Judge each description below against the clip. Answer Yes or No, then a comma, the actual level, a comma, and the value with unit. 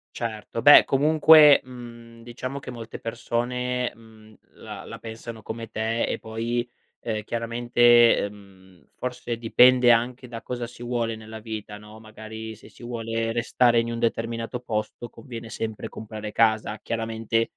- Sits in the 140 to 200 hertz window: No, low, 115 Hz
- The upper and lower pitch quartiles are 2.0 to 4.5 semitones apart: No, narrow, 1.5 semitones